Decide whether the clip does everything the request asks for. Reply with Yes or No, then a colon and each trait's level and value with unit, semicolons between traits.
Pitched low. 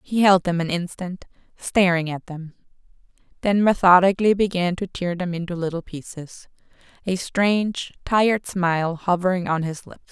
No: medium, 180 Hz